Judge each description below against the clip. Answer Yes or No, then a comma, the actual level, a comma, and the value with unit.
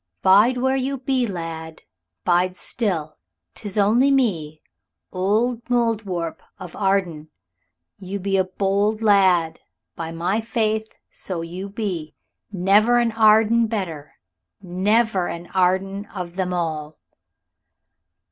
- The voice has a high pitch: Yes, high, 195 Hz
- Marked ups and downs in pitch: No, average, 4.0 semitones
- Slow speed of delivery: Yes, slow, 115 wpm